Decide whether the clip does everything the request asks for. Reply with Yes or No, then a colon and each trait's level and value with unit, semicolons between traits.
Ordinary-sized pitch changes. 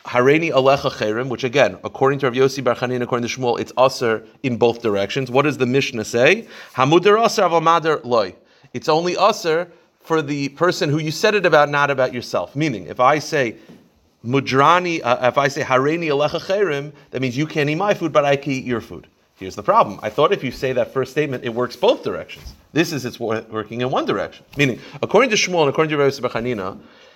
Yes: average, 3.7 semitones